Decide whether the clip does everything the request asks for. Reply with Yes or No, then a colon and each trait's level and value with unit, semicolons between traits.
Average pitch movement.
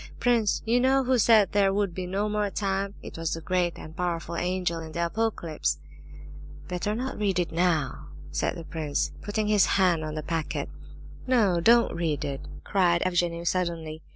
Yes: average, 3.8 semitones